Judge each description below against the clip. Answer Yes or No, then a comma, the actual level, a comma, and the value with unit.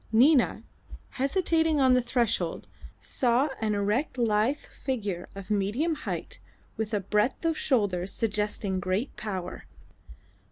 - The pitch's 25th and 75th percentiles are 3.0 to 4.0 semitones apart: No, average, 4.8 semitones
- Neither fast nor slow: No, slow, 120 wpm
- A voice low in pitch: No, high, 225 Hz